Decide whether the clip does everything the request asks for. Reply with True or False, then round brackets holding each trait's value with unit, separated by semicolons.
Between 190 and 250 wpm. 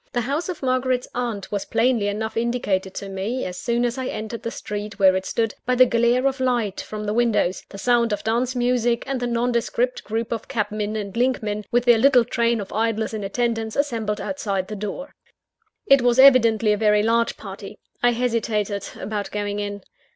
True (195 wpm)